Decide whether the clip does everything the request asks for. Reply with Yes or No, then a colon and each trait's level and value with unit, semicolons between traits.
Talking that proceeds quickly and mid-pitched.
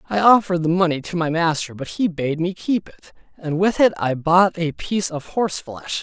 Yes: fast, 230 wpm; medium, 170 Hz